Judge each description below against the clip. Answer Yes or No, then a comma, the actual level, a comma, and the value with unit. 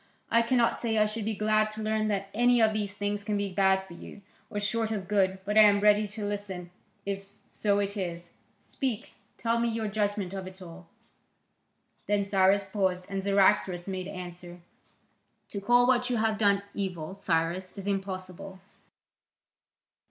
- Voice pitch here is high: Yes, high, 200 Hz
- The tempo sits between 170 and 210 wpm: Yes, average, 175 wpm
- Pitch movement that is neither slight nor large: No, narrow, 2.2 semitones